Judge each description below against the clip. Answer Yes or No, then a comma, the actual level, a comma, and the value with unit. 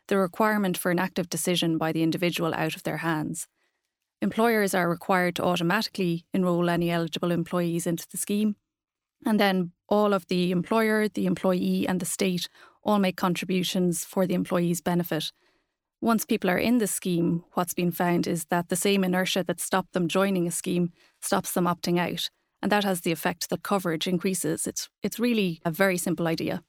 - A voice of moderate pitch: Yes, medium, 180 Hz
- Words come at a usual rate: Yes, average, 185 wpm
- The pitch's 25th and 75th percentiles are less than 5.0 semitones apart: Yes, narrow, 2.4 semitones